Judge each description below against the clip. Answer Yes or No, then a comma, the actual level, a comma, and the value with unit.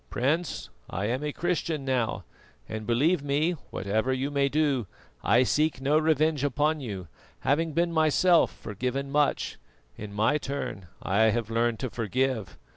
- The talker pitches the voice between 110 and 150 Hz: Yes, low, 135 Hz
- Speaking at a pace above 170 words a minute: No, average, 155 wpm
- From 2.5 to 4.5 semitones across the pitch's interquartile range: No, average, 4.9 semitones